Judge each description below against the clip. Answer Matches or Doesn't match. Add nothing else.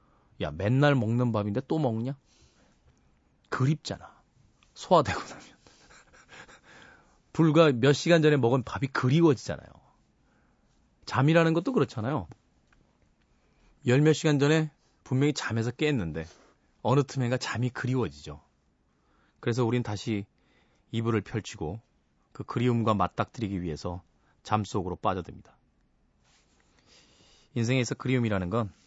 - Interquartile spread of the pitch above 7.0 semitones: Matches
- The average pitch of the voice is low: Matches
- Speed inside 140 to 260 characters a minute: Matches